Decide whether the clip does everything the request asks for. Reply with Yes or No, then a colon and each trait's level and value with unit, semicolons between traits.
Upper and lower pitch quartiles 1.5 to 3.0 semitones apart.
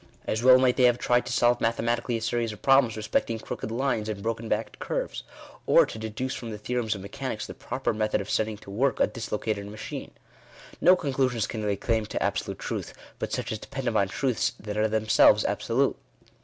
Yes: narrow, 2.4 semitones